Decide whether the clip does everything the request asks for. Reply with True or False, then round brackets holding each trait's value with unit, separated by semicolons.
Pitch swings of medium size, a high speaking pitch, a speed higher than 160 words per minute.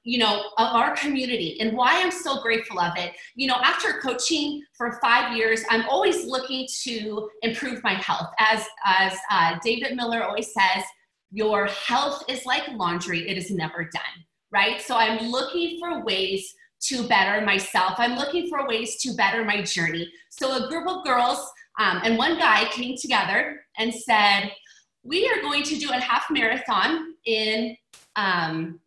True (4.9 semitones; 230 Hz; 170 wpm)